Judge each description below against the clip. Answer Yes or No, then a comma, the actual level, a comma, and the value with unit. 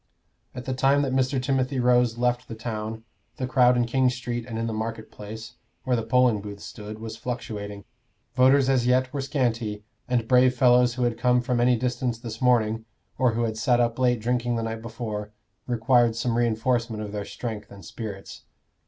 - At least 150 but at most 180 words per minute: No, average, 195 wpm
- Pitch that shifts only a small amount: Yes, narrow, 2.0 semitones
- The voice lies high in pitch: No, low, 120 Hz